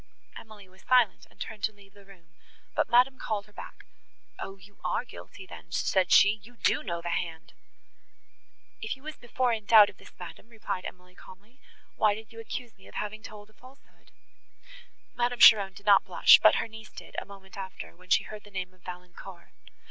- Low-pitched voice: No, high, 205 Hz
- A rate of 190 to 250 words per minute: Yes, average, 200 wpm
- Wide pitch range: No, average, 3.0 semitones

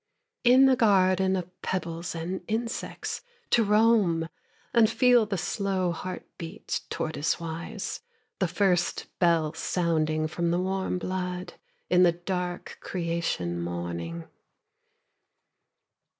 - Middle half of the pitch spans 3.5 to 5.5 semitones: No, average, 2.7 semitones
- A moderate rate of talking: No, slow, 110 wpm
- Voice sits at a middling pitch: Yes, medium, 180 Hz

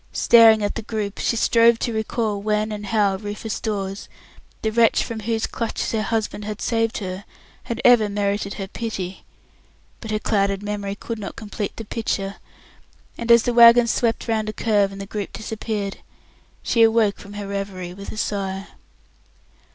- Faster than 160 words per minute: Yes, average, 175 wpm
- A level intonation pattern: Yes, narrow, 2.2 semitones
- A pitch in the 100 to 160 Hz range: No, high, 215 Hz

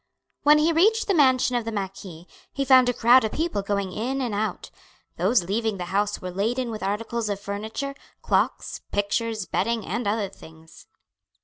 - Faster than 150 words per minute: Yes, average, 180 wpm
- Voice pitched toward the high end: Yes, high, 220 Hz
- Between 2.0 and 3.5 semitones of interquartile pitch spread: No, average, 4.1 semitones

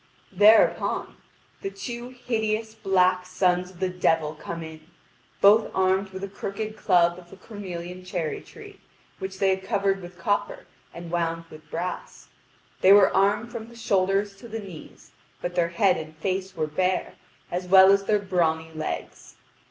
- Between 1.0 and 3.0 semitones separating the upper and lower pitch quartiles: Yes, narrow, 2.6 semitones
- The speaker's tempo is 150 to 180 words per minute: Yes, average, 165 wpm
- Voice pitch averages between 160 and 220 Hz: Yes, high, 190 Hz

